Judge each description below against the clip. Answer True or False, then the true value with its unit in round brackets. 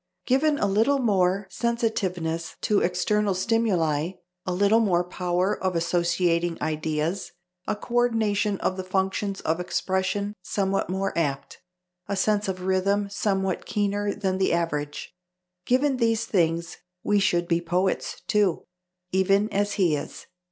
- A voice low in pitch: False (190 Hz)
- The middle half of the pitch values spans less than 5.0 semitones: True (2.9 semitones)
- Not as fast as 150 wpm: True (135 wpm)